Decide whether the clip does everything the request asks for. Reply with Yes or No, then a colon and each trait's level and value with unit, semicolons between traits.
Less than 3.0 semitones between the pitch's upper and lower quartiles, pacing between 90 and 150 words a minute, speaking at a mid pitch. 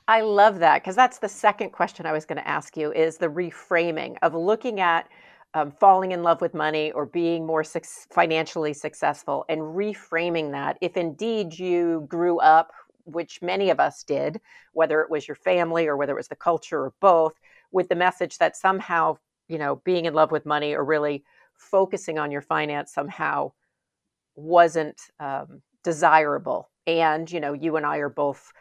No: narrow, 2.4 semitones; average, 185 wpm; medium, 165 Hz